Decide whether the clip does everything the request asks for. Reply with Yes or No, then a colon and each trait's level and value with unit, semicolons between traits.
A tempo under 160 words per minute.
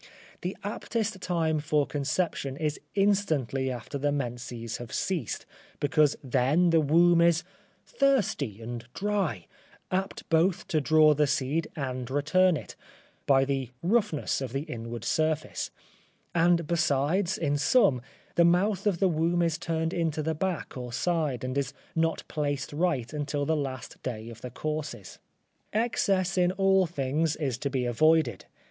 Yes: average, 150 wpm